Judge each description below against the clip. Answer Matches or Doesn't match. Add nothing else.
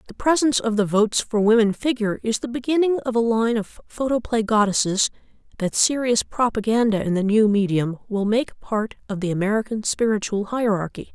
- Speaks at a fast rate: Doesn't match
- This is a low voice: Doesn't match